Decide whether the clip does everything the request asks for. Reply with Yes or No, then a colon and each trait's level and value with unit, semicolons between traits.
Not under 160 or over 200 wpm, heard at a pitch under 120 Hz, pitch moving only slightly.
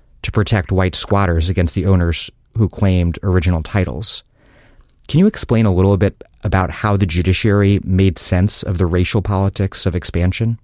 Yes: average, 165 wpm; very low, 95 Hz; narrow, 2.2 semitones